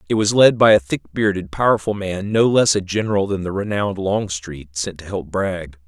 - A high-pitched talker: No, very low, 95 Hz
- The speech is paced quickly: Yes, fast, 215 wpm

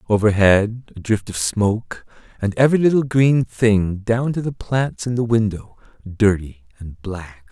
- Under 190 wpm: Yes, average, 160 wpm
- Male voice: Yes, male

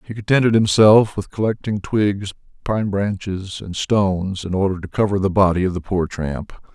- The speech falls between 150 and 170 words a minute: No, average, 180 wpm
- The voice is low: Yes, low, 100 Hz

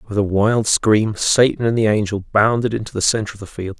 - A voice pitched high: No, low, 105 Hz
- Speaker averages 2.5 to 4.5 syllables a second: No, 5.5 syllables/s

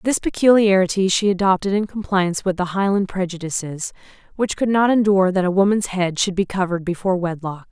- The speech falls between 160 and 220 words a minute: Yes, average, 180 wpm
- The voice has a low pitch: No, high, 190 Hz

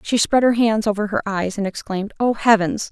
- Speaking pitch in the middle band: No, high, 210 Hz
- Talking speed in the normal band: No, fast, 225 wpm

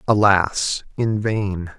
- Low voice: Yes, low, 100 Hz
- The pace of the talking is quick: No, slow, 100 wpm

